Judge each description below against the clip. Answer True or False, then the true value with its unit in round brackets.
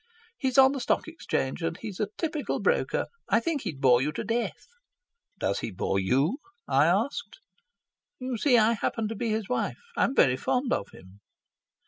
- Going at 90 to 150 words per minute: False (180 wpm)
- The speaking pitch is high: True (220 Hz)